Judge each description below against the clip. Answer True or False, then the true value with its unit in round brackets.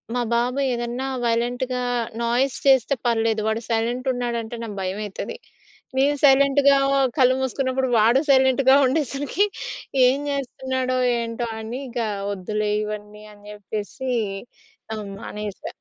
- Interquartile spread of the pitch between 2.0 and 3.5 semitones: True (2.9 semitones)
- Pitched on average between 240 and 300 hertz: True (245 Hz)